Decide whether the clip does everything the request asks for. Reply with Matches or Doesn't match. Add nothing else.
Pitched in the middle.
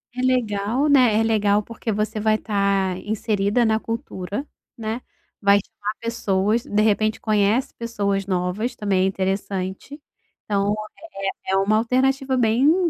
Doesn't match